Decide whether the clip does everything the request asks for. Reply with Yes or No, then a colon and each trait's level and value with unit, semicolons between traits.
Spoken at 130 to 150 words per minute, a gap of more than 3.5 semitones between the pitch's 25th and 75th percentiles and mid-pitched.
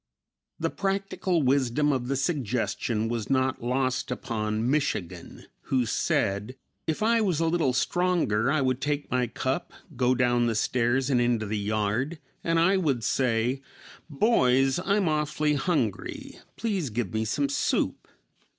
No: average, 145 wpm; average, 4.4 semitones; low, 130 Hz